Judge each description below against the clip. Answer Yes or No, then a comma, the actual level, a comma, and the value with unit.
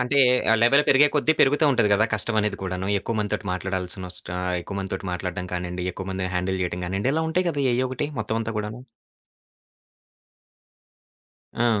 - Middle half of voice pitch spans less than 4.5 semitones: No, average, 5.0 semitones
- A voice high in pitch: No, low, 105 Hz